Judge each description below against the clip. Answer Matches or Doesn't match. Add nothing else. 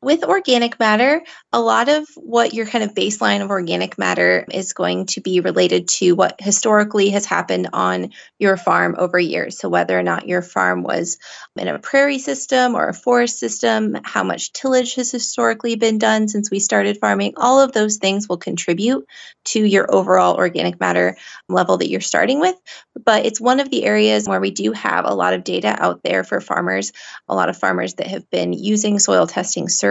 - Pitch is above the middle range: Matches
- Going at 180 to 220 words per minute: Matches